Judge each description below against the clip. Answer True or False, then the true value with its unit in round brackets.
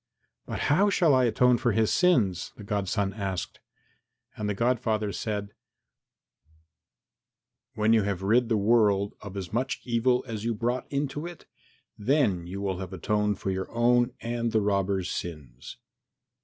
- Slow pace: False (155 wpm)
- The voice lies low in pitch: True (105 Hz)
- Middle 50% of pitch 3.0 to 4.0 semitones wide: True (3.6 semitones)